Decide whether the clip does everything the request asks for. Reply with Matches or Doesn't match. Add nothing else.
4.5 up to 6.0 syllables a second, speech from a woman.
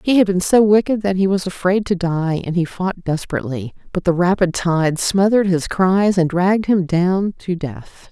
Matches